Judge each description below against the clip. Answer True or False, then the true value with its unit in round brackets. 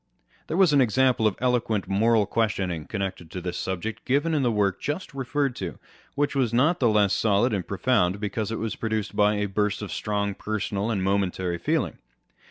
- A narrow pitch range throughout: False (4.0 semitones)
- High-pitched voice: False (105 Hz)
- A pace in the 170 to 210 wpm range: True (195 wpm)